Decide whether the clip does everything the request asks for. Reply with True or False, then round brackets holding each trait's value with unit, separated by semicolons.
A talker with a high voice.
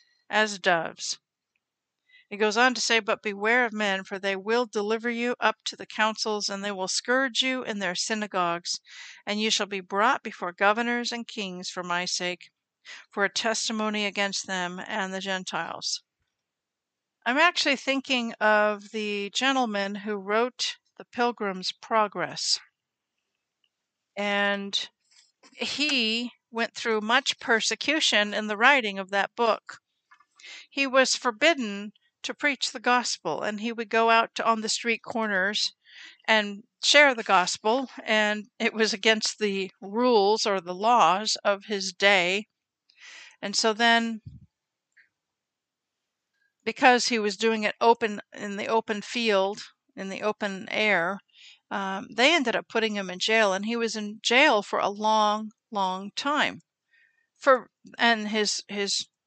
True (220 Hz)